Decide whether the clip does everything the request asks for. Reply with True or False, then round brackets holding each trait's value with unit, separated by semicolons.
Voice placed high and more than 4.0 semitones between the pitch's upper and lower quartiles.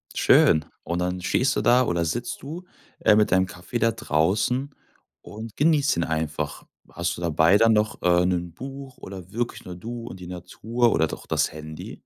False (95 Hz; 5.6 semitones)